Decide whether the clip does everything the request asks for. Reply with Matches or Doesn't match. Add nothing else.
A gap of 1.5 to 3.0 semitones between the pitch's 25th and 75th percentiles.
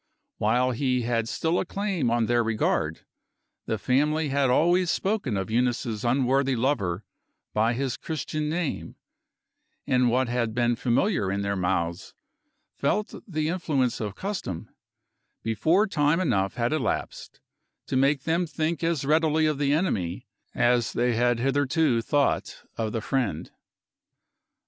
Doesn't match